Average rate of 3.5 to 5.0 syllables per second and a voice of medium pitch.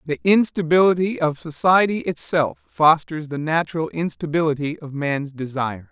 Yes: 4.9 syllables/s; medium, 160 Hz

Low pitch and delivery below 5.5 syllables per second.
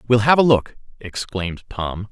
Yes: low, 110 Hz; 4.7 syllables/s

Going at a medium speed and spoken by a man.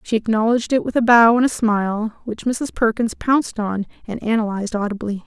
No: average, 195 wpm; female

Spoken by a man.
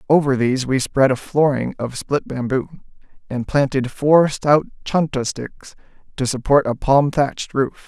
Yes: male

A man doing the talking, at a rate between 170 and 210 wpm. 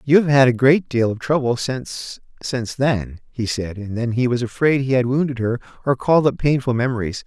Yes: male; fast, 205 wpm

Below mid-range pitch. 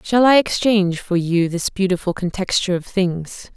No: high, 190 Hz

